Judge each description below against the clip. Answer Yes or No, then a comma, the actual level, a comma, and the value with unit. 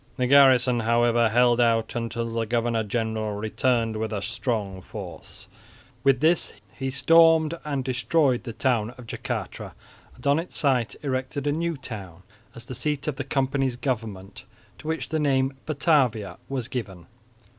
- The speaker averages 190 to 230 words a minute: No, average, 155 wpm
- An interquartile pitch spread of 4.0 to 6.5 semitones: No, average, 3.5 semitones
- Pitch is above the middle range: No, low, 125 Hz